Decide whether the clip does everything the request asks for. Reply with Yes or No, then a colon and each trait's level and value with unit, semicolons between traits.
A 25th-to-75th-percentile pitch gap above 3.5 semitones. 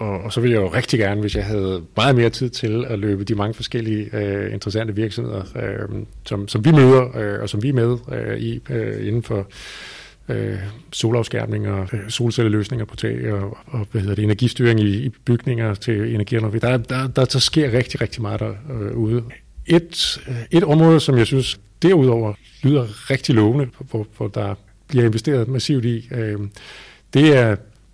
No: average, 3.2 semitones